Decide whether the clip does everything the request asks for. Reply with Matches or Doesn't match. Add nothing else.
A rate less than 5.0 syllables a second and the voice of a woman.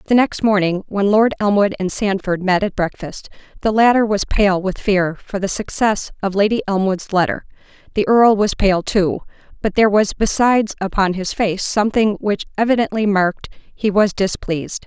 Doesn't match